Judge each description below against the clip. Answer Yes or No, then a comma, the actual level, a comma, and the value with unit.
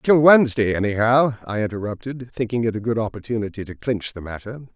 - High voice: No, low, 115 Hz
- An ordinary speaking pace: Yes, average, 175 wpm